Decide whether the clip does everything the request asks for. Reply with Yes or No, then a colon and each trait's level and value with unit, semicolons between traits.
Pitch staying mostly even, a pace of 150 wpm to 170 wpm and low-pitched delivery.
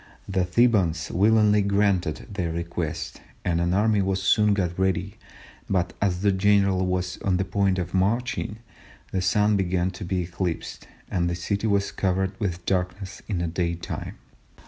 Yes: narrow, 2.3 semitones; average, 165 wpm; very low, 95 Hz